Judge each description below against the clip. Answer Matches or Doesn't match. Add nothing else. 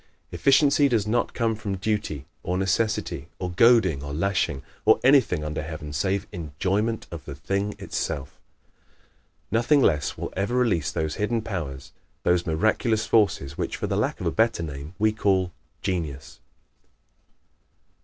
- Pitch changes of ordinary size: Doesn't match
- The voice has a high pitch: Doesn't match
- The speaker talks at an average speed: Matches